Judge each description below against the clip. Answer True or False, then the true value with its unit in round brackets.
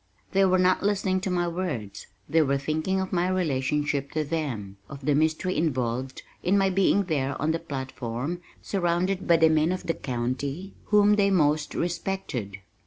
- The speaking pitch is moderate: True (160 Hz)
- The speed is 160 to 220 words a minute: True (175 wpm)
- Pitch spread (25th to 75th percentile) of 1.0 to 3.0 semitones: False (5.1 semitones)